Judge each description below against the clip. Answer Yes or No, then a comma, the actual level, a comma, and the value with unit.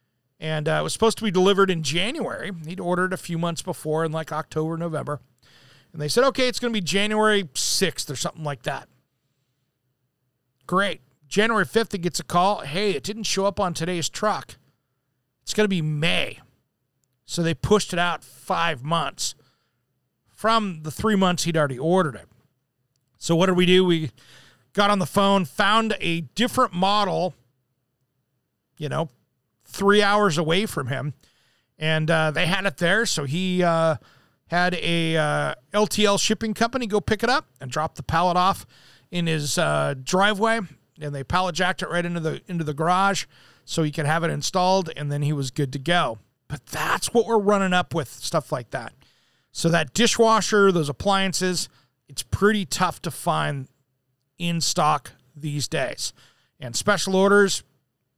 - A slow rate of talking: No, average, 175 wpm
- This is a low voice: No, medium, 165 Hz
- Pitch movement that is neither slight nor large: No, wide, 5.8 semitones